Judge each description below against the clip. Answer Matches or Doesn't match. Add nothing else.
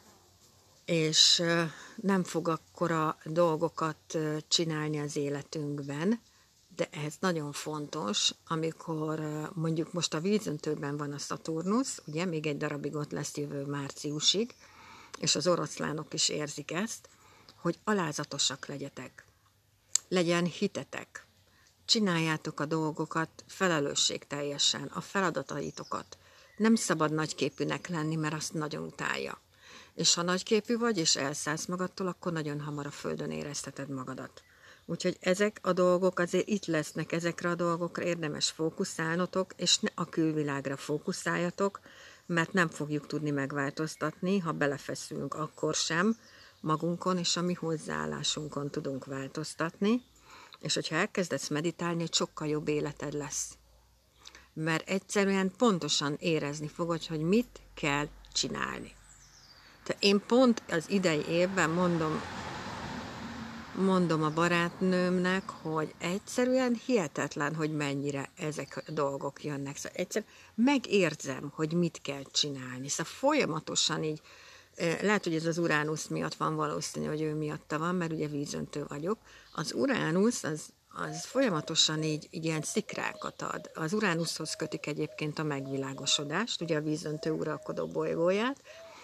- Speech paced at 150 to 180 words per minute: Doesn't match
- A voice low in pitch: Doesn't match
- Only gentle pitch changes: Doesn't match